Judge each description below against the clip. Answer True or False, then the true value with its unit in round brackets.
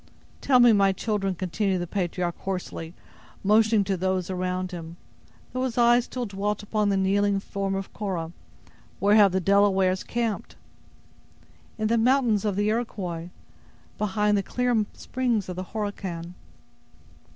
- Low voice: False (200 Hz)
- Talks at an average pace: True (145 wpm)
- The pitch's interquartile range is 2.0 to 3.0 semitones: True (2.7 semitones)